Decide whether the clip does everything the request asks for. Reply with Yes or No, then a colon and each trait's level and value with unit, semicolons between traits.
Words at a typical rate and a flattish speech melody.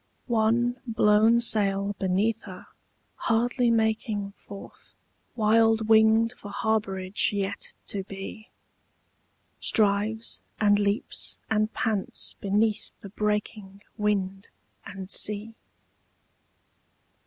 No: slow, 90 wpm; narrow, 1.8 semitones